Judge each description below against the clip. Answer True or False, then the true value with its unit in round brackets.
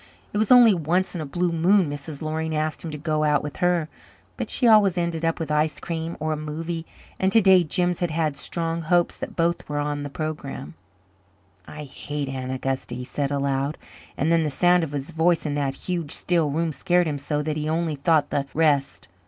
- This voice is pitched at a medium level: True (155 Hz)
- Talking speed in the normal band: False (220 wpm)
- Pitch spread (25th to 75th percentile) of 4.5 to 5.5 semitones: False (2.7 semitones)